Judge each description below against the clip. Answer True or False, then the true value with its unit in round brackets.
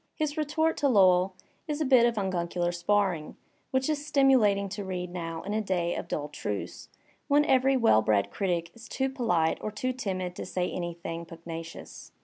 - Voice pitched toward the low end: False (195 Hz)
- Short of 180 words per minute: False (185 wpm)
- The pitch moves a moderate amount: False (7.2 semitones)